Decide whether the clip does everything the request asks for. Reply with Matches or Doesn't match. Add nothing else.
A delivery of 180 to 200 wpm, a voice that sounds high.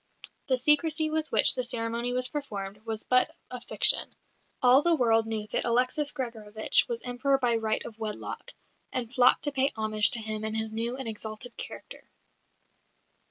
Doesn't match